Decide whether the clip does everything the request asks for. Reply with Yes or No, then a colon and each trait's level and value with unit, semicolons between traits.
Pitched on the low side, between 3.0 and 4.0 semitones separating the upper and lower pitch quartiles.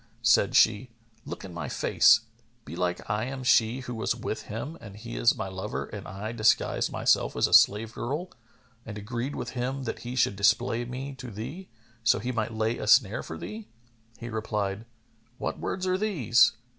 Yes: low, 115 Hz; average, 3.3 semitones